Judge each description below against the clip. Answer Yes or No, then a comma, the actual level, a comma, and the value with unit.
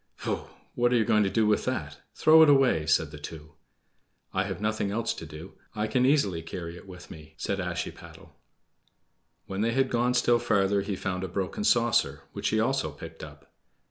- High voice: No, low, 100 Hz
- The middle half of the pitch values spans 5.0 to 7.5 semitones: Yes, wide, 5.4 semitones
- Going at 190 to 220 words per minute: Yes, average, 200 wpm